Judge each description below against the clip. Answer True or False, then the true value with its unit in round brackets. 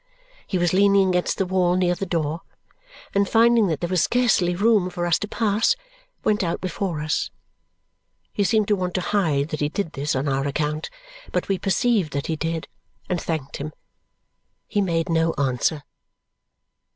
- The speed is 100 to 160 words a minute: False (175 wpm)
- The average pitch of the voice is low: False (180 Hz)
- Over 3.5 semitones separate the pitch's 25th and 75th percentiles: True (4.2 semitones)